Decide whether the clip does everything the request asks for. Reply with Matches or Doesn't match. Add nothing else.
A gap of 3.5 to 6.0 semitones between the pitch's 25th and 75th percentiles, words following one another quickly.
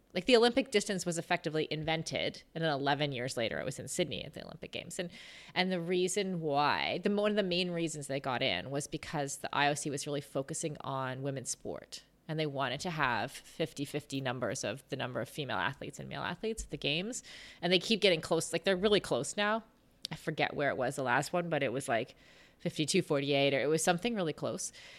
Matches